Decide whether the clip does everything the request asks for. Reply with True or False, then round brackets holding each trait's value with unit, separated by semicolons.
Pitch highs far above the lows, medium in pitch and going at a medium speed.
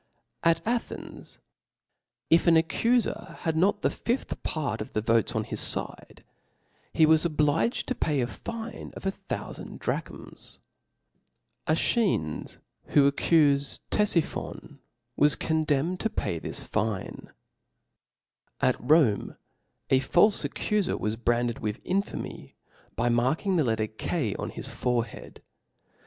False (7.3 semitones; 150 Hz; 130 wpm)